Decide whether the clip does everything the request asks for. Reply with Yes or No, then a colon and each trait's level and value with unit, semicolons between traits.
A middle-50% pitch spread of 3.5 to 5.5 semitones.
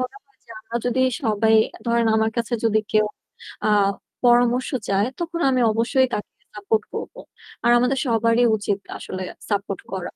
No: average, 2.7 semitones